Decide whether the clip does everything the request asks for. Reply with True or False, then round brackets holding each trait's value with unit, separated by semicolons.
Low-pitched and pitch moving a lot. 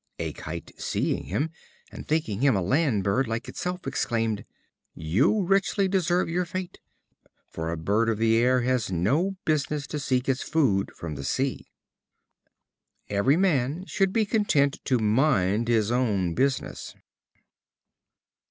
True (130 Hz; 7.4 semitones)